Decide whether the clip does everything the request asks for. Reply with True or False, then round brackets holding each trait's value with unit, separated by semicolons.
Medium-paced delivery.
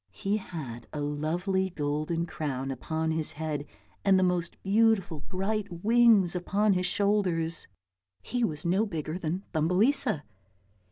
False (130 wpm)